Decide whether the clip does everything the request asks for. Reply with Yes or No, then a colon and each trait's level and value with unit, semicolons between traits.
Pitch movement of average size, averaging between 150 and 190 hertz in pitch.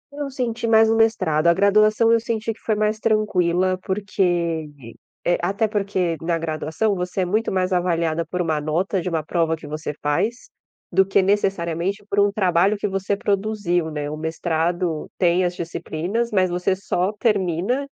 Yes: average, 3.8 semitones; medium, 185 Hz